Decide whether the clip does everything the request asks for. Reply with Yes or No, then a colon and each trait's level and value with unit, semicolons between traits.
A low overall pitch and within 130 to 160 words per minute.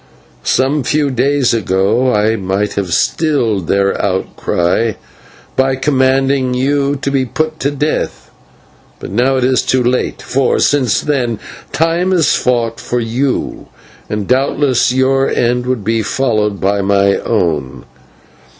Yes: low, 125 Hz; slow, 135 wpm